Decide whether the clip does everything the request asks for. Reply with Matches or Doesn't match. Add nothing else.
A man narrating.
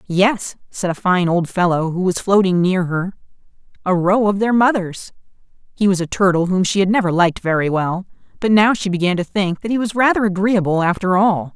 Doesn't match